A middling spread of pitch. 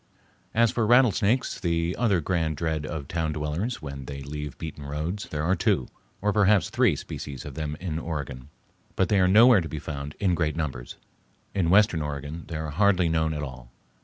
Yes: average, 4.6 semitones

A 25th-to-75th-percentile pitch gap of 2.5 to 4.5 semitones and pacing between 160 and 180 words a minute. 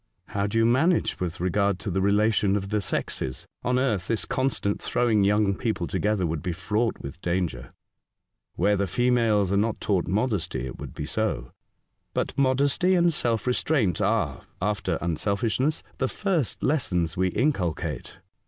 No: average, 5.0 semitones; average, 165 wpm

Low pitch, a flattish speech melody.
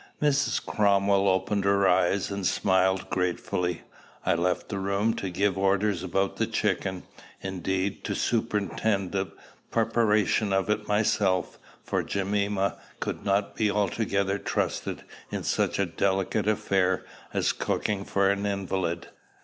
Yes: low, 100 Hz; narrow, 1.4 semitones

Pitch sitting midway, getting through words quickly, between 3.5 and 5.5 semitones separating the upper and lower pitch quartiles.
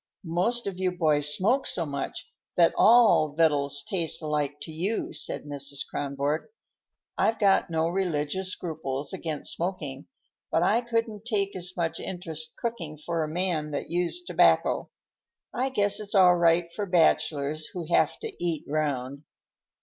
No: medium, 165 Hz; average, 150 wpm; average, 4.3 semitones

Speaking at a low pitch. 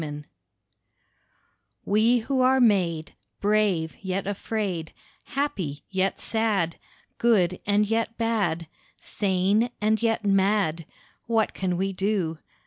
No: high, 200 Hz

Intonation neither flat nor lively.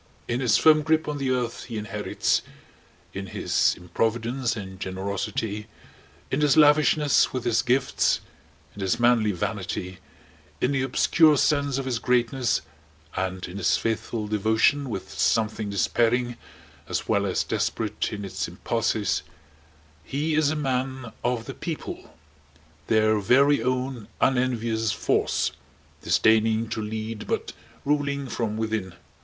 Yes: average, 3.9 semitones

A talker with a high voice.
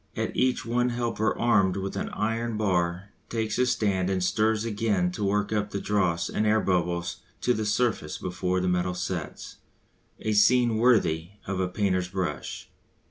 No: low, 100 Hz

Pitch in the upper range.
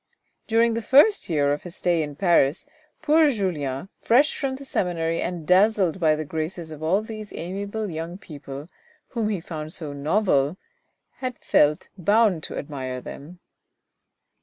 No: medium, 175 Hz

